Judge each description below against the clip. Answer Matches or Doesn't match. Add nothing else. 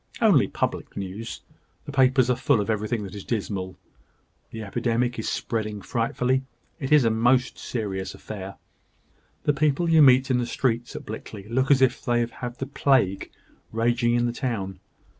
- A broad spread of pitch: Doesn't match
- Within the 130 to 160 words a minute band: Doesn't match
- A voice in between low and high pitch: Doesn't match